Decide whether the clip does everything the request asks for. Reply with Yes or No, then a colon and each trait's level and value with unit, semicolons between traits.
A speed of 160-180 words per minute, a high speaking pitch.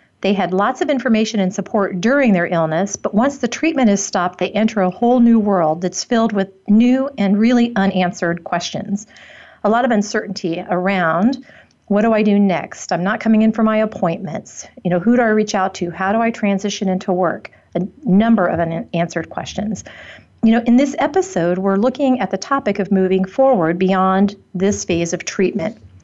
No: average, 195 wpm; high, 200 Hz